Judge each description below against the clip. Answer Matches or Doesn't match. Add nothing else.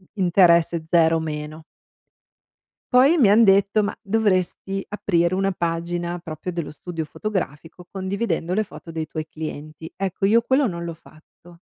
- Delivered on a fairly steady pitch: Doesn't match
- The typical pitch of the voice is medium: Matches